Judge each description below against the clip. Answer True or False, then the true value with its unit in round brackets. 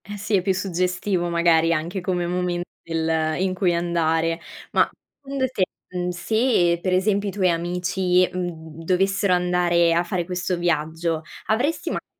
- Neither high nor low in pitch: True (180 Hz)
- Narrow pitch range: True (1.8 semitones)